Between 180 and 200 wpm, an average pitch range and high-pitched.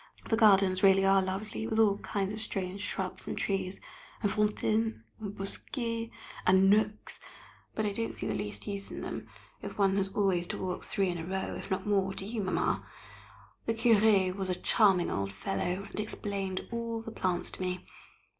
No: average, 190 wpm; narrow, 2.2 semitones; high, 195 Hz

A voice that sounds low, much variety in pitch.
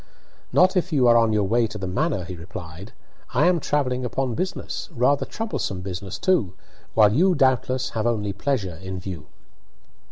Yes: low, 115 Hz; wide, 6.4 semitones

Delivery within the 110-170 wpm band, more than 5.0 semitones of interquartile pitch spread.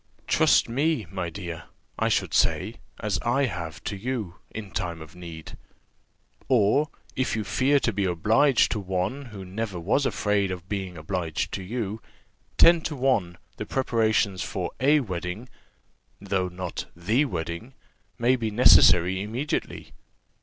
Yes: average, 145 wpm; wide, 5.4 semitones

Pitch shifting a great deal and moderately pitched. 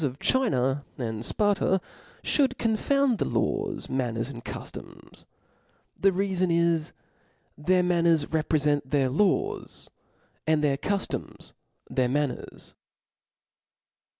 Yes: wide, 6.3 semitones; medium, 160 Hz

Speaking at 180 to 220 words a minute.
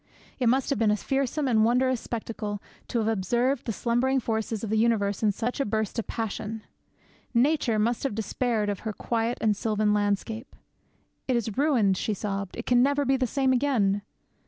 Yes: average, 190 wpm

